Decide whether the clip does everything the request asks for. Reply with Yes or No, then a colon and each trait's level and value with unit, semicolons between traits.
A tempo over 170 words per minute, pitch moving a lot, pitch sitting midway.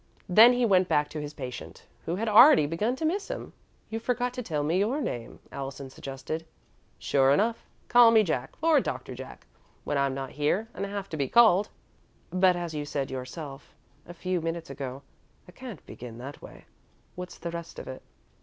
Yes: average, 190 wpm; wide, 7.8 semitones; medium, 170 Hz